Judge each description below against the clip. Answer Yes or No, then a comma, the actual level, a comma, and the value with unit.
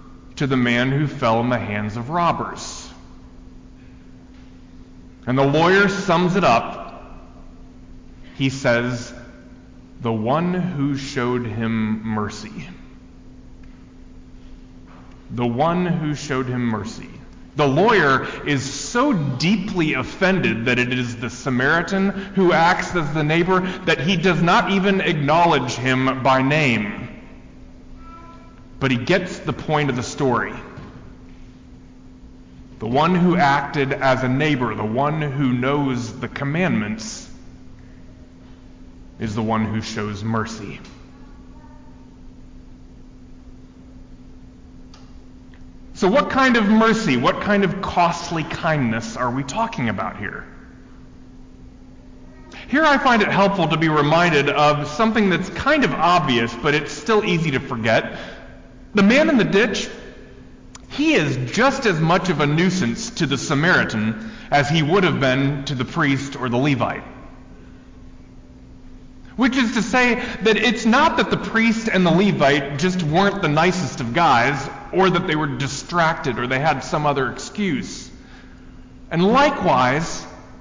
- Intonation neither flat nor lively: No, wide, 7.5 semitones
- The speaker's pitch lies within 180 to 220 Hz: No, medium, 140 Hz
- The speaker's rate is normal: No, slow, 130 wpm